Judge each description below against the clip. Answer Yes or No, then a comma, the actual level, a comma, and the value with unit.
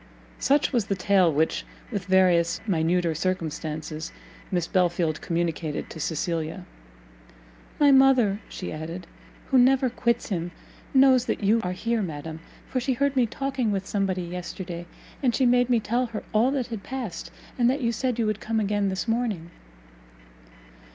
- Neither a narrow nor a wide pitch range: No, wide, 6.0 semitones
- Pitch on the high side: Yes, high, 200 Hz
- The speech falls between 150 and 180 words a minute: Yes, average, 160 wpm